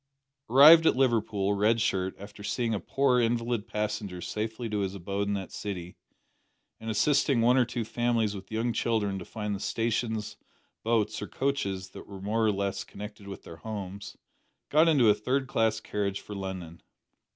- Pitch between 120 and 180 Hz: No, low, 105 Hz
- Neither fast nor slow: Yes, average, 175 wpm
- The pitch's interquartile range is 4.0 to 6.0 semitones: No, average, 3.0 semitones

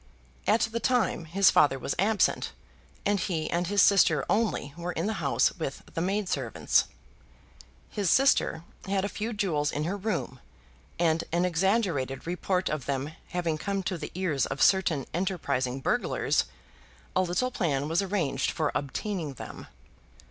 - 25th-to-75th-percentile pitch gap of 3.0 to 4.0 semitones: No, average, 5.0 semitones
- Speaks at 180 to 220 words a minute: No, average, 155 wpm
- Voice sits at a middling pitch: Yes, medium, 175 Hz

